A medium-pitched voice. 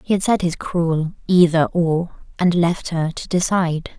Yes: medium, 170 Hz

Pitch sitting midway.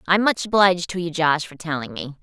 Yes: medium, 170 Hz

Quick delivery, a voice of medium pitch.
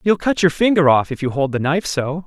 Yes: fast, 290 wpm; medium, 160 Hz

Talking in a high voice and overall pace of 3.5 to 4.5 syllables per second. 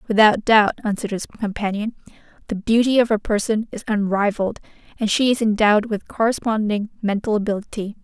No: high, 215 Hz; 5.9 syllables/s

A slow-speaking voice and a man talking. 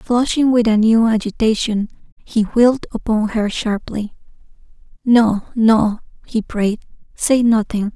No: slow, 120 wpm; female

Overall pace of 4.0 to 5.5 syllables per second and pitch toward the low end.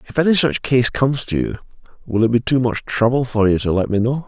No: 6.1 syllables/s; low, 125 Hz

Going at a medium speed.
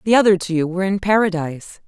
Yes: average, 195 wpm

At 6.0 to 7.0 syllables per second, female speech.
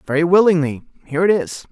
No: 6.5 syllables/s; male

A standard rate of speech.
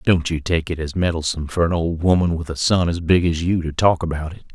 No: fast, 275 wpm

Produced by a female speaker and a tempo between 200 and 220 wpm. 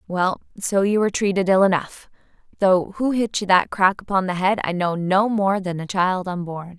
Yes: female; fast, 205 wpm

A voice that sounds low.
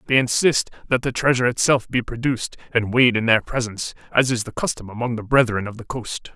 Yes: low, 120 Hz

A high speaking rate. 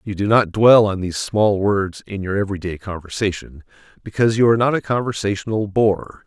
No: average, 180 wpm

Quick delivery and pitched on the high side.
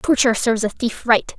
Yes: fast, 215 wpm; high, 235 Hz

